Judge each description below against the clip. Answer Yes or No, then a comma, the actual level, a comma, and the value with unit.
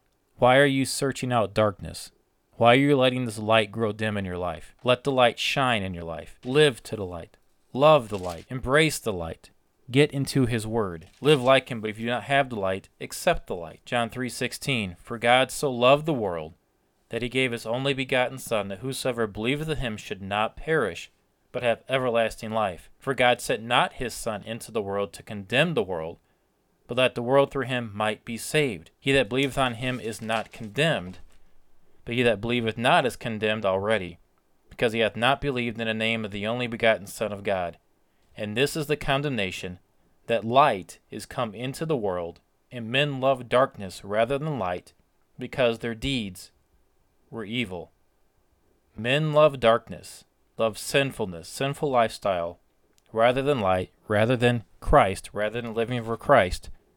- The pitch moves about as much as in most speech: Yes, average, 4.2 semitones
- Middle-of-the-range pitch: No, low, 115 Hz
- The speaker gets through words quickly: No, average, 185 wpm